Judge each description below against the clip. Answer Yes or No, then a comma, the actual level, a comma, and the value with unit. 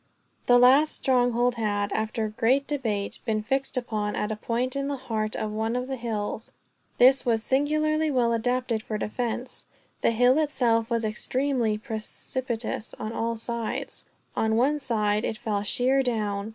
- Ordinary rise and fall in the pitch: Yes, average, 3.0 semitones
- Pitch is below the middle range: No, high, 235 Hz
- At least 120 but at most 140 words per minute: No, average, 165 wpm